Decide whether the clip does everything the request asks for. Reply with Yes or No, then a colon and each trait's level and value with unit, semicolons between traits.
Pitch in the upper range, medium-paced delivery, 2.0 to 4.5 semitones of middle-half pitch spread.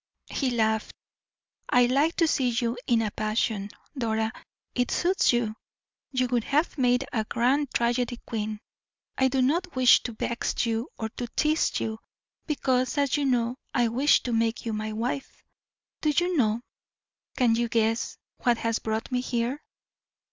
Yes: high, 240 Hz; average, 160 wpm; average, 2.8 semitones